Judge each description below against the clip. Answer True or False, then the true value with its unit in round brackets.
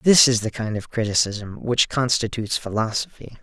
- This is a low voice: True (115 Hz)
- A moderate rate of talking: True (160 wpm)